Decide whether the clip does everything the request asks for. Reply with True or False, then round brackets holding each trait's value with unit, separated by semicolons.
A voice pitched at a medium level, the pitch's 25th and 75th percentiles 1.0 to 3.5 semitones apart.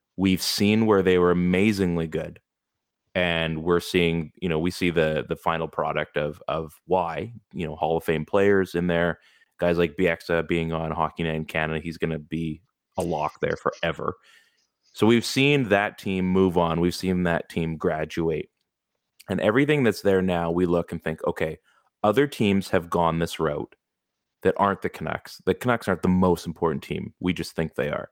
False (85 Hz; 2.4 semitones)